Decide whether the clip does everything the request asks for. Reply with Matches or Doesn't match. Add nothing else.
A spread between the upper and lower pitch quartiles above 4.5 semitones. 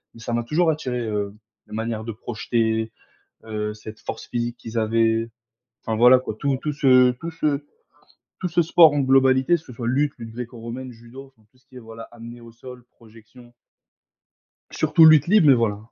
Doesn't match